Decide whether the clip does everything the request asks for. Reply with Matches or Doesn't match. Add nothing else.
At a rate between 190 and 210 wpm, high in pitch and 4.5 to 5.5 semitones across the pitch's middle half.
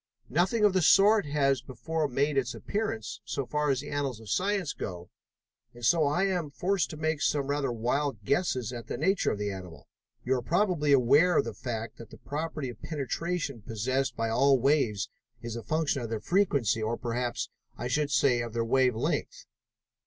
Doesn't match